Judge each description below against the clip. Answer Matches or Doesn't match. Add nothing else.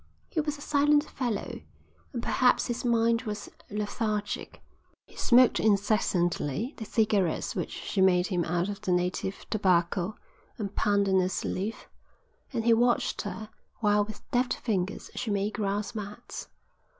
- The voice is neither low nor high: Doesn't match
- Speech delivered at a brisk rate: Doesn't match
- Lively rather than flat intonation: Doesn't match